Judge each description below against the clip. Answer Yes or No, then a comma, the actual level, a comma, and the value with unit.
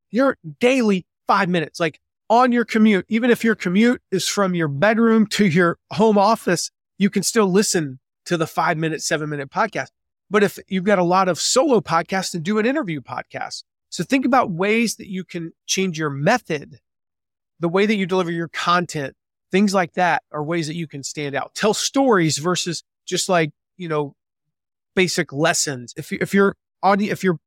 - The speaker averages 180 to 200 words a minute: Yes, average, 190 wpm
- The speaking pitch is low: No, medium, 185 Hz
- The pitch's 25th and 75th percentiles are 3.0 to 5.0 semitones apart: Yes, average, 4.3 semitones